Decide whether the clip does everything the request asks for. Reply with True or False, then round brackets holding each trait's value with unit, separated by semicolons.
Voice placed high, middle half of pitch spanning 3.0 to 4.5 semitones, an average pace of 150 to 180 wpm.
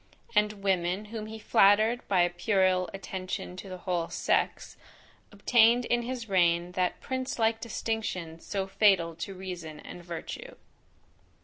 False (195 Hz; 3.8 semitones; 140 wpm)